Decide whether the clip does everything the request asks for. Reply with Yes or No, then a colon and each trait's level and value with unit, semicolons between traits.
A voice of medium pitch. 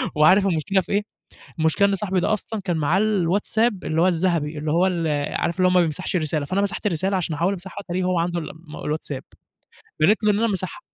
Yes: medium, 180 Hz